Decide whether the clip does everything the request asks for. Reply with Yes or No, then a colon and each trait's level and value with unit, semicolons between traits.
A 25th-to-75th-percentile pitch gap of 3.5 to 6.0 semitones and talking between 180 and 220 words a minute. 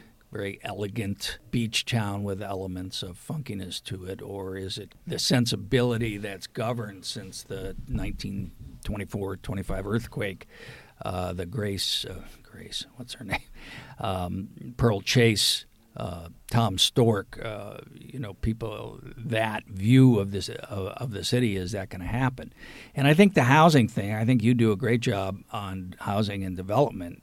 No: average, 4.1 semitones; average, 150 wpm